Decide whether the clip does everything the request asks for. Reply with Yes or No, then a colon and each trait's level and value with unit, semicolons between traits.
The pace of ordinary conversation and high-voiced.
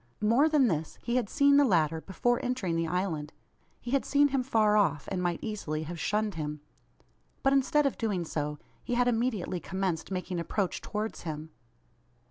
Yes: average, 180 wpm; high, 200 Hz